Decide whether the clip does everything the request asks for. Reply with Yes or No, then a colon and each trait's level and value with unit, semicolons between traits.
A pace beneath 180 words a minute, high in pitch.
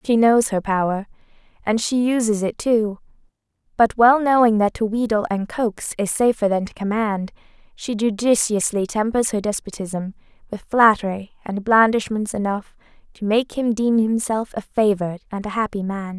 Yes: average, 160 wpm; high, 215 Hz